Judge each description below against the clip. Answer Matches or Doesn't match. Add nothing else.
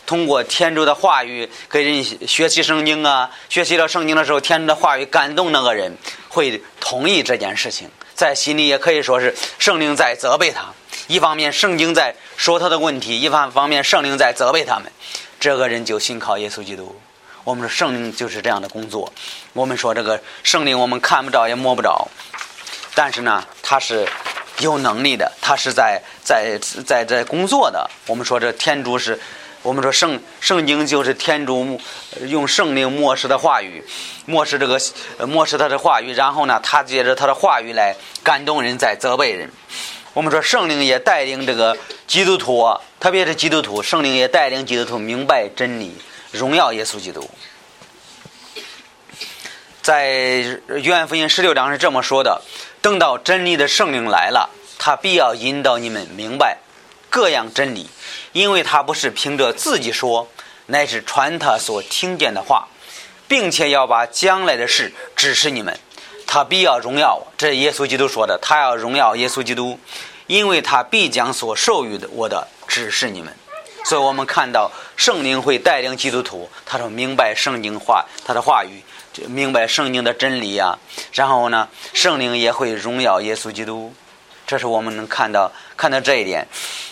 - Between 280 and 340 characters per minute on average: Doesn't match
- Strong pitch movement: Doesn't match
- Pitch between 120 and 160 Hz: Matches